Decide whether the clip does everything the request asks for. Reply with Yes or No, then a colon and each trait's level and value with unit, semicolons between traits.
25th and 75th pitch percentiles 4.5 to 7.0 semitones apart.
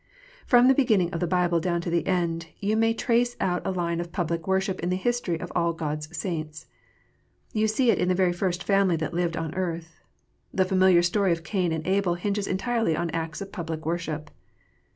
No: average, 2.7 semitones